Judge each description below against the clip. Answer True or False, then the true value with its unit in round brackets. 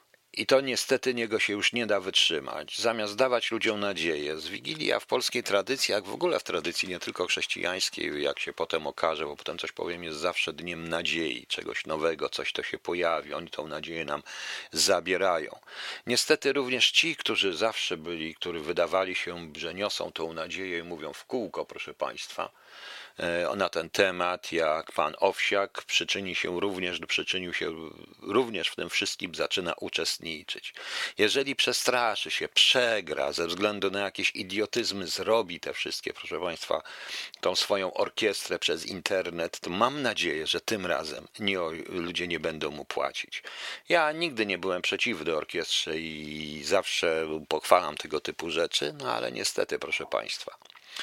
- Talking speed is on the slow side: False (155 wpm)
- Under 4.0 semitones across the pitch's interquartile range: False (5.4 semitones)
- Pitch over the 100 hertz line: False (95 Hz)